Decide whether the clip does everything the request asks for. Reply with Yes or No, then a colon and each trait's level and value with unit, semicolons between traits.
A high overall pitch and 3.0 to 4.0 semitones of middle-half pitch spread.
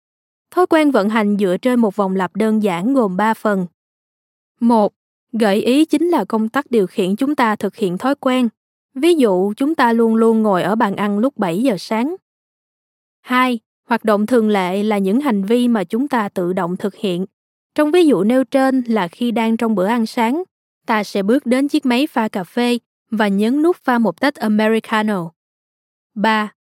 Yes: high, 225 Hz; average, 3.7 semitones